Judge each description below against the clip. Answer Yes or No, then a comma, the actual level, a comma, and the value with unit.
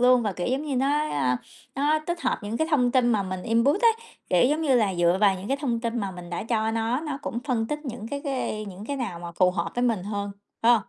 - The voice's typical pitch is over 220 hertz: Yes, high, 230 Hz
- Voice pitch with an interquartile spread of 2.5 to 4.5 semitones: No, wide, 5.6 semitones